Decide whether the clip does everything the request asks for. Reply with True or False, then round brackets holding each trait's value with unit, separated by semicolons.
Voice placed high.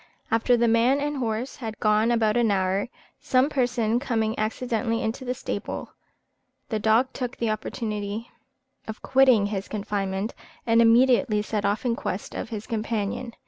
True (225 Hz)